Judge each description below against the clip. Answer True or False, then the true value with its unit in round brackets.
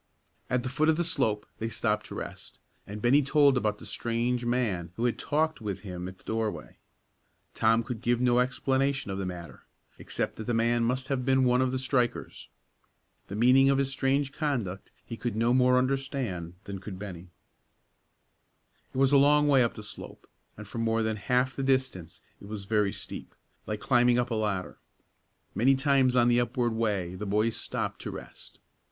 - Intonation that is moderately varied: True (3.8 semitones)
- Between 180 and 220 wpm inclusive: True (195 wpm)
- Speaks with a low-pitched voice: True (120 Hz)